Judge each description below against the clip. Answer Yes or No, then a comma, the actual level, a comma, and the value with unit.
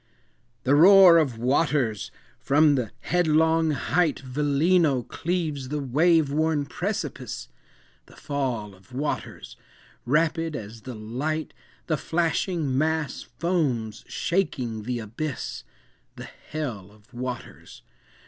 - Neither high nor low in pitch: Yes, medium, 145 Hz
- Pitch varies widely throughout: No, average, 4.7 semitones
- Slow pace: Yes, slow, 105 wpm